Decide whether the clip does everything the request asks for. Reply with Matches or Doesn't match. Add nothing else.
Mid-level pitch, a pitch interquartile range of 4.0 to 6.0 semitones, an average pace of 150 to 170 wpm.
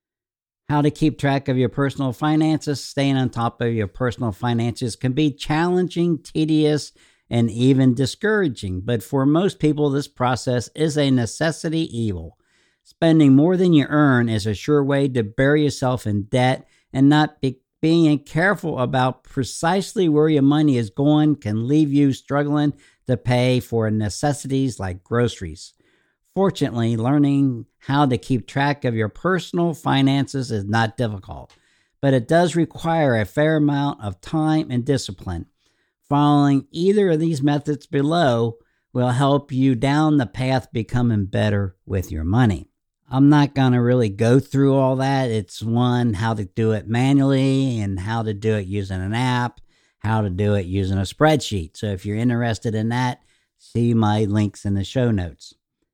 Doesn't match